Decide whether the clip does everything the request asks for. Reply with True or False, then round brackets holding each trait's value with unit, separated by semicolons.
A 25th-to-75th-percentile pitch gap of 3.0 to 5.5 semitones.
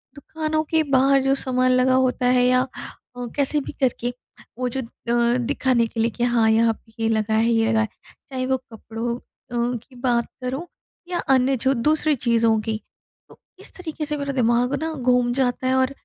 False (2.4 semitones)